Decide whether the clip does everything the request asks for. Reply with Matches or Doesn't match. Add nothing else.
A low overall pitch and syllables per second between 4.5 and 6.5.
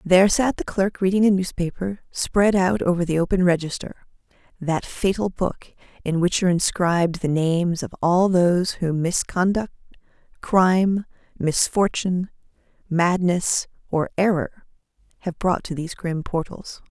Doesn't match